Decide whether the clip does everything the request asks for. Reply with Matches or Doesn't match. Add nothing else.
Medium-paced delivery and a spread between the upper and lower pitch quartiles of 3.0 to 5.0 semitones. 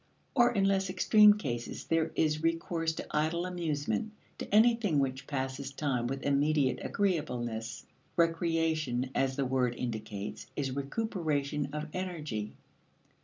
Doesn't match